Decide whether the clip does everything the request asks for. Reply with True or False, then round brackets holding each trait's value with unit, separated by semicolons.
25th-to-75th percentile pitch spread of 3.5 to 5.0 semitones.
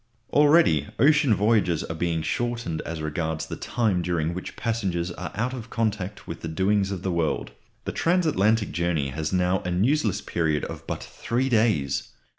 False (5.6 semitones)